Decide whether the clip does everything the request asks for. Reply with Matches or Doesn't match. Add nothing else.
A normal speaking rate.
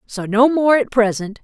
Doesn't match